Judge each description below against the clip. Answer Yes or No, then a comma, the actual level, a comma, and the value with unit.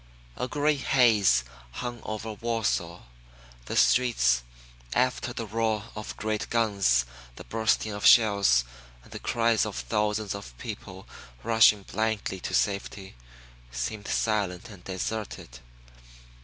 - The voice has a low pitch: Yes, low, 105 Hz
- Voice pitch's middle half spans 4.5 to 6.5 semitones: No, average, 2.9 semitones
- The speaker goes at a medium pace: No, slow, 120 wpm